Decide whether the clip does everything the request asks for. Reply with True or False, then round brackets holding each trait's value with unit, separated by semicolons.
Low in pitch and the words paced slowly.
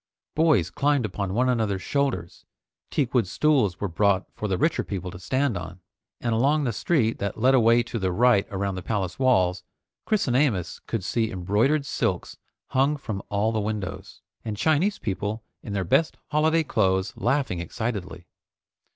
False (110 Hz; 170 wpm)